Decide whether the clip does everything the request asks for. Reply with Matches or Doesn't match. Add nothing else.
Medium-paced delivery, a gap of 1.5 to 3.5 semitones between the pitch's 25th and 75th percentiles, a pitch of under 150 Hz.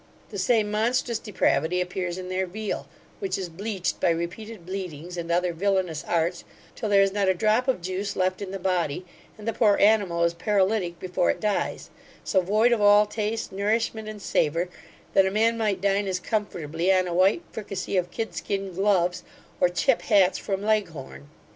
Doesn't match